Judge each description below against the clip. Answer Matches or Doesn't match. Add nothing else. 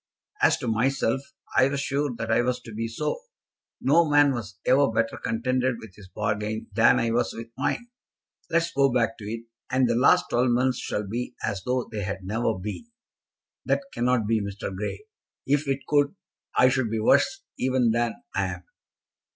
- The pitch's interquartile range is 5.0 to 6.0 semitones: Doesn't match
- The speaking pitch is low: Matches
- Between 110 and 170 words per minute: Doesn't match